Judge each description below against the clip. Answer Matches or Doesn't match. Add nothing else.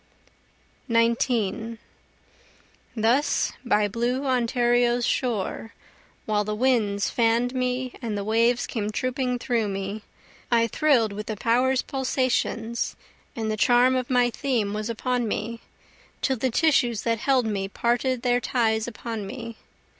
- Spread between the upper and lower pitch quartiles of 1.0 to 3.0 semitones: Matches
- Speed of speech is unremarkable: Doesn't match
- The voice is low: Doesn't match